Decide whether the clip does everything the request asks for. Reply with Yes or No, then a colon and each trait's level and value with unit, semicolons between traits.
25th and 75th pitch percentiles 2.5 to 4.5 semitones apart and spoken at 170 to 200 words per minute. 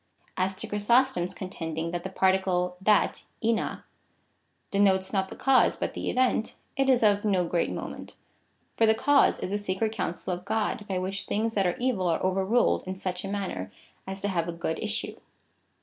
Yes: average, 3.0 semitones; average, 185 wpm